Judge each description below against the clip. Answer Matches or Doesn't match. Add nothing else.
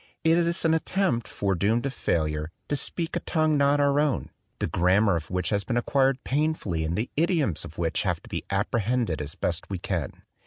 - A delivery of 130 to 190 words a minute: Doesn't match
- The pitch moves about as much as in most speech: Doesn't match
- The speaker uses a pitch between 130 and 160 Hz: Doesn't match